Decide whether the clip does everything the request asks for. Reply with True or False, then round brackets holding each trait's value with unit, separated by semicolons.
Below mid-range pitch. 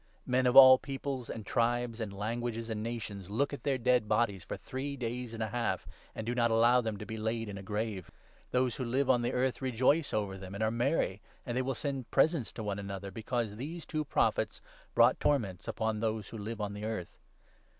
True (115 Hz)